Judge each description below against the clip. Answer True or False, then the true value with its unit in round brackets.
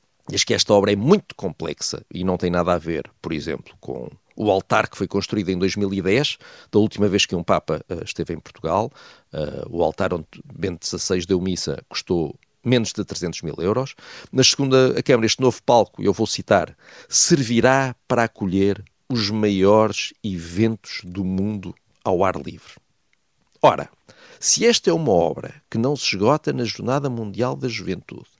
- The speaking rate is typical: True (175 wpm)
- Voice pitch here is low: True (105 Hz)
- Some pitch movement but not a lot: True (4.5 semitones)